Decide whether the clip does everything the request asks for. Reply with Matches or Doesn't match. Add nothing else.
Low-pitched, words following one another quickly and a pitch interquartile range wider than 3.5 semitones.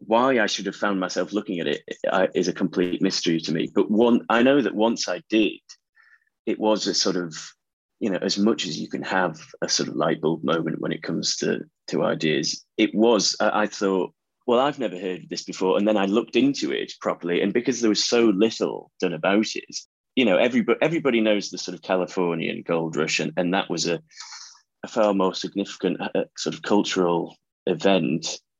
Matches